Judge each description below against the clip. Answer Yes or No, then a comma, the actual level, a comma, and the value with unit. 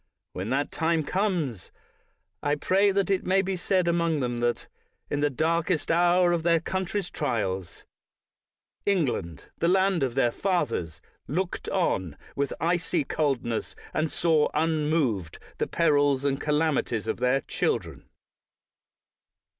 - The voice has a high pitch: No, medium, 155 Hz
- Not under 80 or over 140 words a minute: Yes, slow, 135 wpm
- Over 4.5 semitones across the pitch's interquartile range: Yes, average, 5.2 semitones